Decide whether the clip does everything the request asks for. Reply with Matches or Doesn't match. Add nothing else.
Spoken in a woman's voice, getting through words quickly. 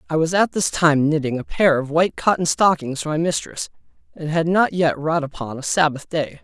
Doesn't match